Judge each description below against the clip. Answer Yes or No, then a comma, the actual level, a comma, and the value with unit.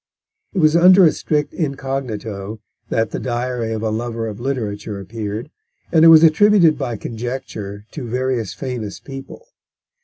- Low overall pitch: Yes, low, 125 Hz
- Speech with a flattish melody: No, average, 5.3 semitones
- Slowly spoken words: No, average, 150 wpm